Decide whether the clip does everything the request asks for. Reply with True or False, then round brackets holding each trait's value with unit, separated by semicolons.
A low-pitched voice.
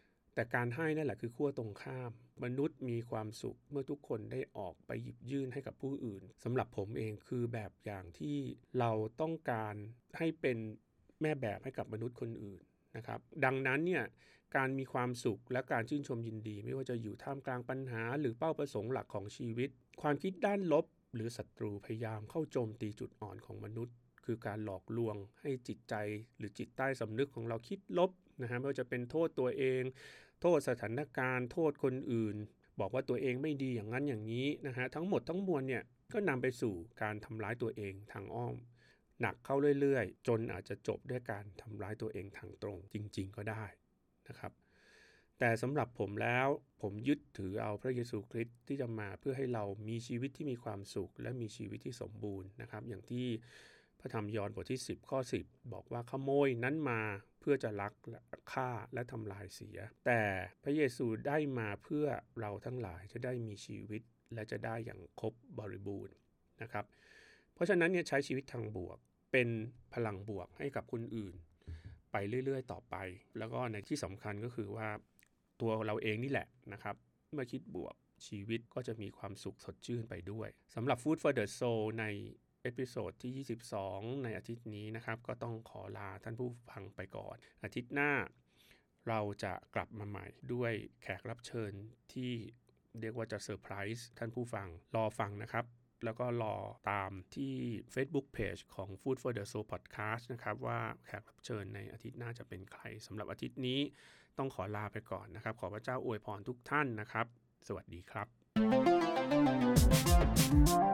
True (115 Hz)